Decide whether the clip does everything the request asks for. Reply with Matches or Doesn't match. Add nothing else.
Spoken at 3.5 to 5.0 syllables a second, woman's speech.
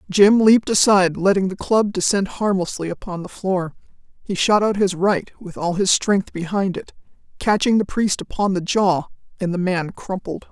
Matches